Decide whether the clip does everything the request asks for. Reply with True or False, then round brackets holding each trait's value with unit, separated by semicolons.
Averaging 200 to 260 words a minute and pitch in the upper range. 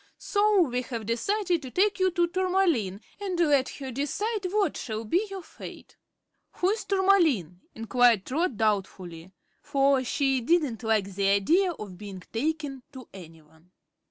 False (150 wpm; 270 Hz)